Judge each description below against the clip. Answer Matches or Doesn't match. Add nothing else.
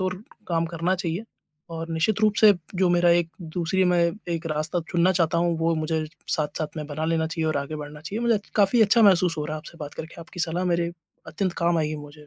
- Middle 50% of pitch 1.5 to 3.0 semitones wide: Matches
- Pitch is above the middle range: Doesn't match